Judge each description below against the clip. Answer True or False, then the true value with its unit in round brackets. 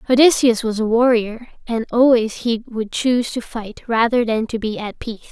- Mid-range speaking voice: False (230 Hz)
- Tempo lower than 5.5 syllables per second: True (5.2 syllables/s)